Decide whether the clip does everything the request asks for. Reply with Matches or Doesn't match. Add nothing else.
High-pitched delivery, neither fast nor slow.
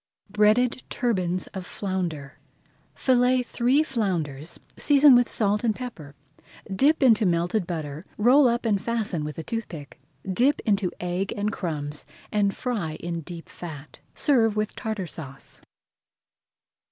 Doesn't match